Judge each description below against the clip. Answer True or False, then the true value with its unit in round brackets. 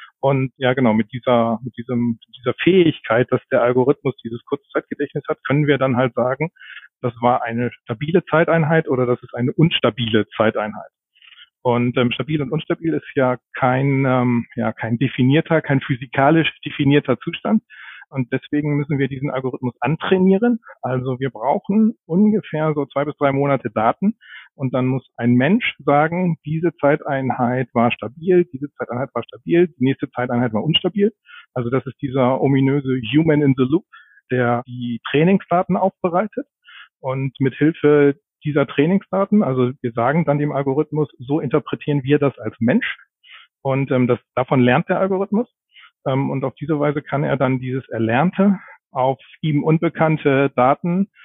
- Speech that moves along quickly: False (155 wpm)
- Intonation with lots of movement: False (4.0 semitones)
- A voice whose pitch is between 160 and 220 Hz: False (140 Hz)